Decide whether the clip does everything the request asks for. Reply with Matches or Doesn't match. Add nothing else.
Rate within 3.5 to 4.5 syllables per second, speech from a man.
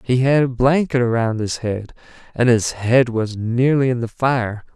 Matches